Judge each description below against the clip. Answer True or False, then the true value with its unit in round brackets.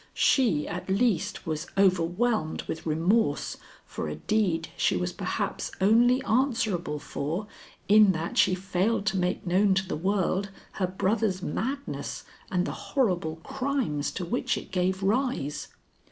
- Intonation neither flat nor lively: True (4.3 semitones)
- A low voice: False (190 Hz)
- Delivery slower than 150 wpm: True (140 wpm)